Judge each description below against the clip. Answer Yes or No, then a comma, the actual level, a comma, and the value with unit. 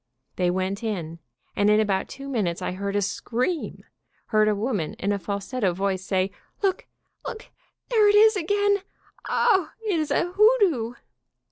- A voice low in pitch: No, high, 220 Hz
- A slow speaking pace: No, average, 160 wpm